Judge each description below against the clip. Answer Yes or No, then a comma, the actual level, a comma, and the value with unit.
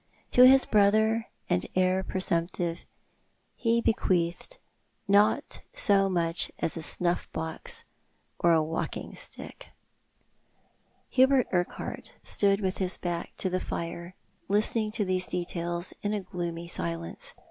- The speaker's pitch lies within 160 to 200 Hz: Yes, medium, 185 Hz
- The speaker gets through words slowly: Yes, slow, 125 wpm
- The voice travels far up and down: No, average, 3.4 semitones